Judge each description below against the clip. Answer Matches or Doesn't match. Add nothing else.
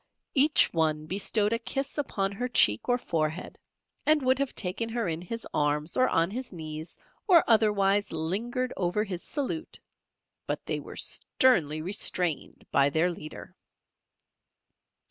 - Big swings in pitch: Matches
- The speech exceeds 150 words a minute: Doesn't match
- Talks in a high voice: Matches